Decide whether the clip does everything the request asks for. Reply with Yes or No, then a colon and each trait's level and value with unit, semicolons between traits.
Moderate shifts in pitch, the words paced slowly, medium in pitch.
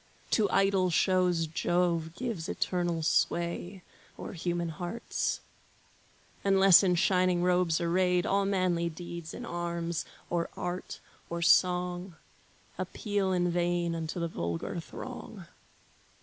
No: narrow, 1.5 semitones; slow, 115 wpm; medium, 175 Hz